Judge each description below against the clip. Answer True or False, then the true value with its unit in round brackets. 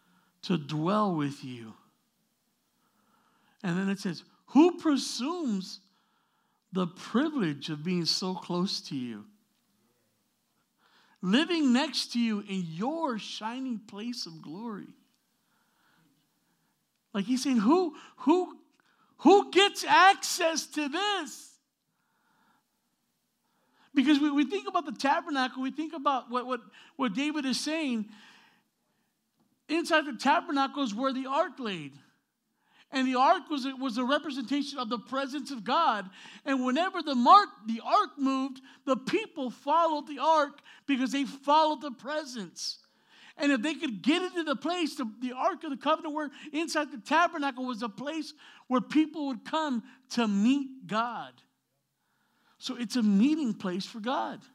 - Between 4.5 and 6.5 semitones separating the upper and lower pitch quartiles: True (5.1 semitones)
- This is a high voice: True (265 Hz)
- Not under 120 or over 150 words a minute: True (140 wpm)